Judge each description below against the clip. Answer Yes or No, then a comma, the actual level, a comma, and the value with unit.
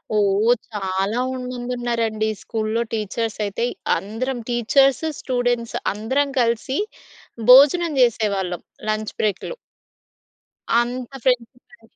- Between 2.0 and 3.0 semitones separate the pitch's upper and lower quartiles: Yes, average, 2.7 semitones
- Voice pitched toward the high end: Yes, high, 230 Hz